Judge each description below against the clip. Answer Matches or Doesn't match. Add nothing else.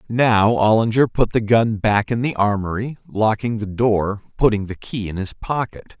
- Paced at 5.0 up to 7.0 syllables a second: Doesn't match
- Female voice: Doesn't match